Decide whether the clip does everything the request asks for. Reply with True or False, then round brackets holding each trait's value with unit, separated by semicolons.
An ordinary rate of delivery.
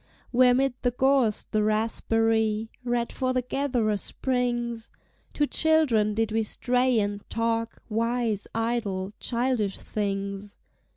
False (120 wpm)